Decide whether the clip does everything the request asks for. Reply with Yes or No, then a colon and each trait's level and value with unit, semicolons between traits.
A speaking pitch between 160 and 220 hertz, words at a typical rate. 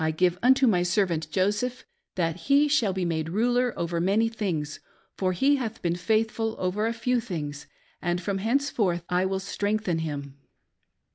Yes: high, 190 Hz; average, 160 wpm